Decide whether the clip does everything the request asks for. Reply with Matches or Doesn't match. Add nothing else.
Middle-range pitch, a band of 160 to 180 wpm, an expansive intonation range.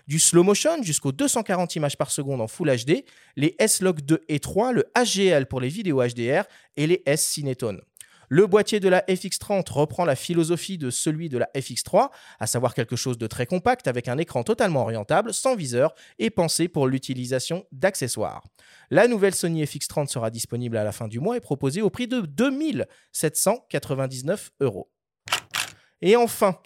Matches